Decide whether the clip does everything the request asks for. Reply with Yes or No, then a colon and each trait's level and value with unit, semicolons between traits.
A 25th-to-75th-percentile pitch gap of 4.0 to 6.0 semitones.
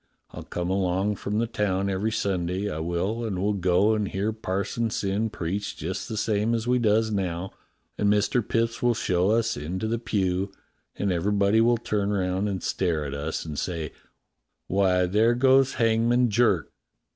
No: average, 3.4 semitones